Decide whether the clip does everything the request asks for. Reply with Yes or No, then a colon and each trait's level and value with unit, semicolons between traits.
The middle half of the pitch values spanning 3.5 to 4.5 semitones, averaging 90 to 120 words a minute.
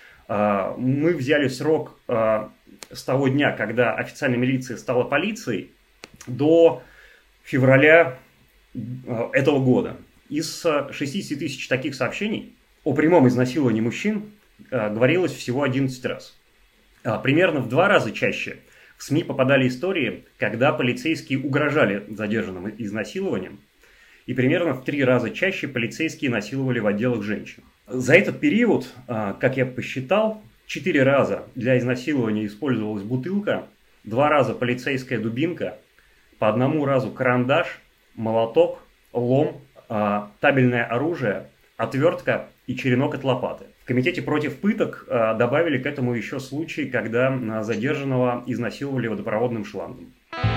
Yes: average, 3.8 semitones; average, 115 wpm